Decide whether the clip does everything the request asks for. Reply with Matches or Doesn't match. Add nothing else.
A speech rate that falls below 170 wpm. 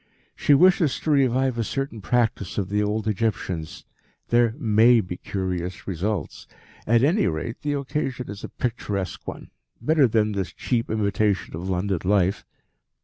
Matches